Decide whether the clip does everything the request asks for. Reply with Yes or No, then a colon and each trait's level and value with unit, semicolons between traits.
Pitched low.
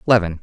Yes: very low, 95 Hz